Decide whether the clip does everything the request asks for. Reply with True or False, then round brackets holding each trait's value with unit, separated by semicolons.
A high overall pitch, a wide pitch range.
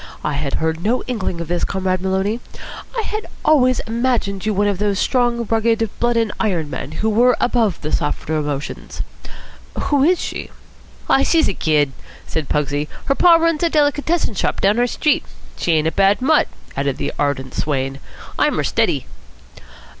True (205 Hz; 8.0 semitones)